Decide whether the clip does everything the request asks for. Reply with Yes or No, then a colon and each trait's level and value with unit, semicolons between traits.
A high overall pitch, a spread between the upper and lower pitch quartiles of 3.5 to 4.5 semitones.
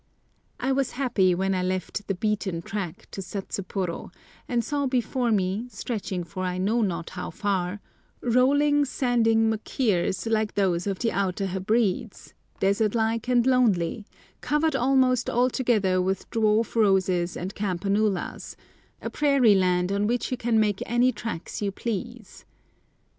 Yes: high, 210 Hz; average, 4.2 semitones